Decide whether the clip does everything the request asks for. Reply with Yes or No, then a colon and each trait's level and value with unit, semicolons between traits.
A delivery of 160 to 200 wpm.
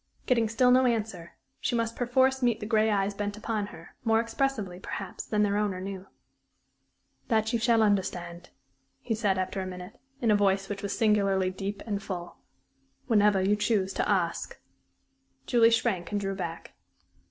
Yes: average, 170 wpm